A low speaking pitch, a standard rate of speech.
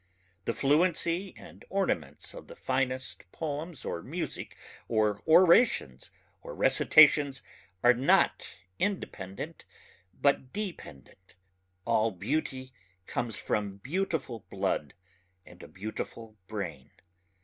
No: low, 130 Hz; slow, 100 wpm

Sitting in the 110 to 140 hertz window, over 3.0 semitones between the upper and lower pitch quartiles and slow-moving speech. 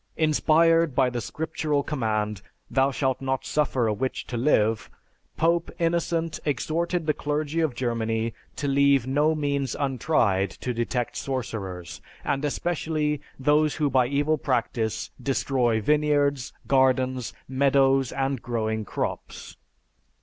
Yes: low, 135 Hz; average, 3.8 semitones; slow, 125 wpm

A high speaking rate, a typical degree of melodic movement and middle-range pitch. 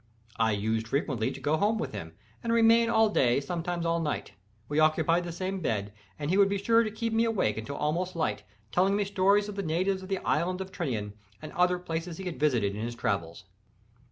No: fast, 225 wpm; wide, 7.0 semitones; medium, 170 Hz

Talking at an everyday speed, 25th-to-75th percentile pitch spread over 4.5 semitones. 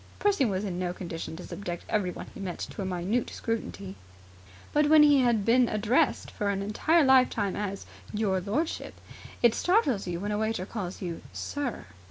Yes: average, 180 wpm; average, 5.2 semitones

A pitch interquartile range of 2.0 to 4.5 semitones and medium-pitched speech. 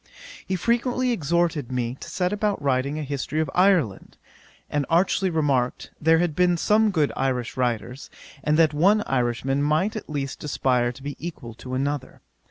No: average, 5.3 semitones; medium, 150 Hz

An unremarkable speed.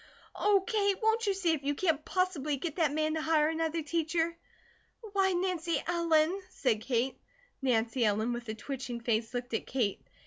Yes: average, 180 wpm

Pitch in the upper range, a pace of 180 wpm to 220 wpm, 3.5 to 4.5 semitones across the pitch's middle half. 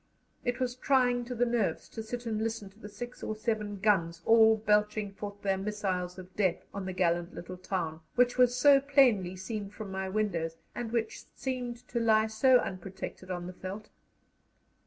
Yes: high, 210 Hz; average, 185 wpm; average, 4.2 semitones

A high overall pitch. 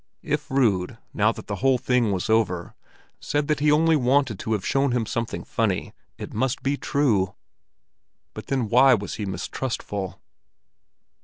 No: low, 120 Hz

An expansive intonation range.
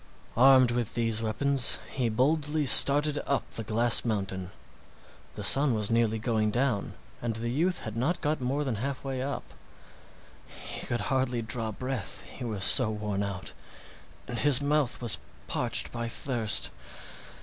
No: average, 3.8 semitones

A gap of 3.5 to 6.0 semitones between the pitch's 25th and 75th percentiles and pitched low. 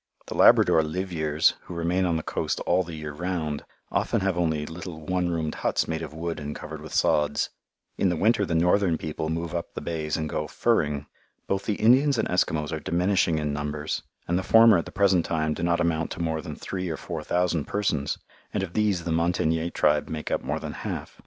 No: average, 2.7 semitones; very low, 85 Hz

